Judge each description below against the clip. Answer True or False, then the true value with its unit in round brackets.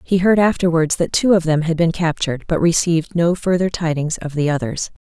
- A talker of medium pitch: True (165 Hz)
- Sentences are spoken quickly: True (215 wpm)